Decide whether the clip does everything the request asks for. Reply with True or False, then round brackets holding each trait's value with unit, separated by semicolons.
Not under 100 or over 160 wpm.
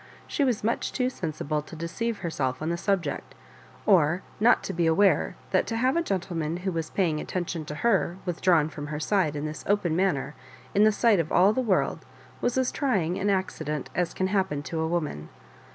False (200 wpm)